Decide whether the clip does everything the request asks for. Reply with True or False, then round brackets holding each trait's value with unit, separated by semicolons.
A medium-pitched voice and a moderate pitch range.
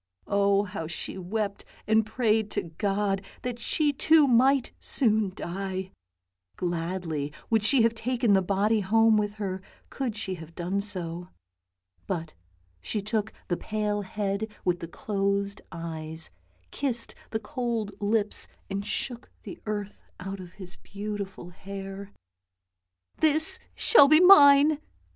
False (205 Hz; 3.2 semitones)